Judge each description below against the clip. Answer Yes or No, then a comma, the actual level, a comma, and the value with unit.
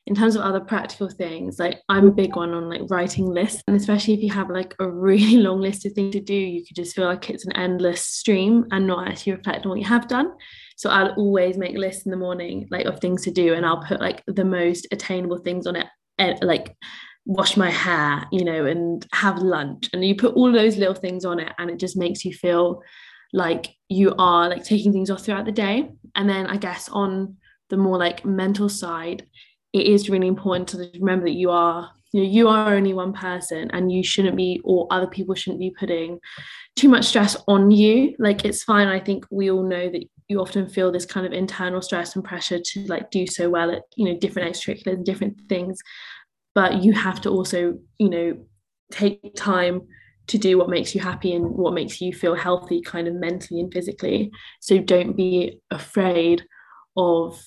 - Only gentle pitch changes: Yes, narrow, 2.1 semitones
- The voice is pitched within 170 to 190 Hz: Yes, medium, 185 Hz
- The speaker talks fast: Yes, fast, 220 wpm